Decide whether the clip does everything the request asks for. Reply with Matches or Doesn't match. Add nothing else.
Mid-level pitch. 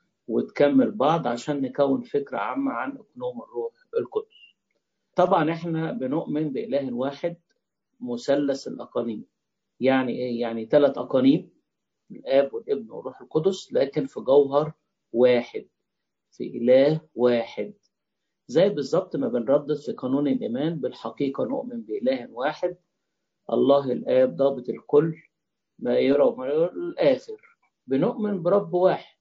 Matches